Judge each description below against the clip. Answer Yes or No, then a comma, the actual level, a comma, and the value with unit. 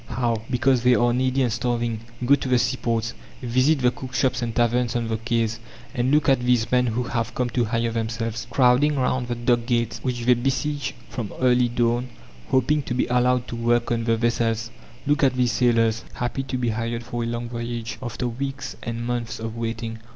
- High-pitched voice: No, low, 120 Hz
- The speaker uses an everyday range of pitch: No, narrow, 1.4 semitones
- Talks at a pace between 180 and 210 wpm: Yes, fast, 205 wpm